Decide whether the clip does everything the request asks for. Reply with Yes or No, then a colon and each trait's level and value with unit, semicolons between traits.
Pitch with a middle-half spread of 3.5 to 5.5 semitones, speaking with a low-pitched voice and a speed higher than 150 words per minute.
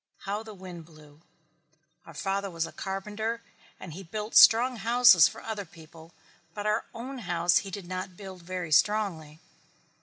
No: average, 4.1 semitones; high, 190 Hz; average, 160 wpm